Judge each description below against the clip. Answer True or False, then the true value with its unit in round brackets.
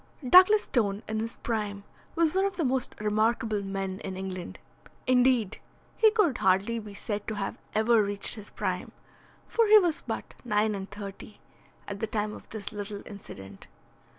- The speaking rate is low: False (170 wpm)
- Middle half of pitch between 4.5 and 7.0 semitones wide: False (3.5 semitones)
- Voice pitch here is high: True (215 Hz)